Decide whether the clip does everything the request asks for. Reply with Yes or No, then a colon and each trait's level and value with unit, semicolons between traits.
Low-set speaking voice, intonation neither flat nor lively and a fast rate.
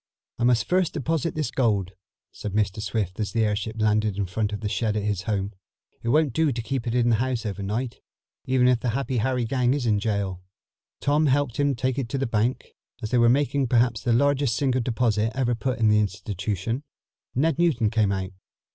Yes: low, 115 Hz; average, 3.7 semitones; fast, 215 wpm